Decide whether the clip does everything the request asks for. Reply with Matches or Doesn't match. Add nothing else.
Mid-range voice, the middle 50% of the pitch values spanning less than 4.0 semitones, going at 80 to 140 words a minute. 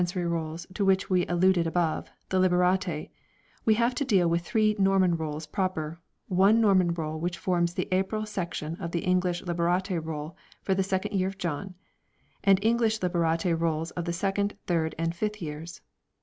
Doesn't match